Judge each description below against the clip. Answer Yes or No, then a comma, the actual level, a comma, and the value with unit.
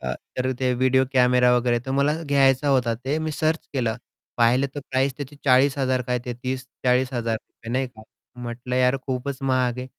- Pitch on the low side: Yes, low, 130 Hz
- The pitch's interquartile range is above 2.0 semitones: No, narrow, 1.5 semitones